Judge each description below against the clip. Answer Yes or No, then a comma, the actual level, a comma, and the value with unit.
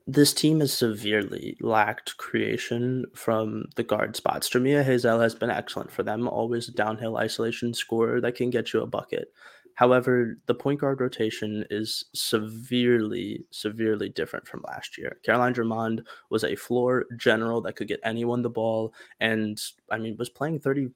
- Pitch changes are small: Yes, narrow, 2.0 semitones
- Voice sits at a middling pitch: No, low, 120 Hz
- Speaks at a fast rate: No, average, 170 wpm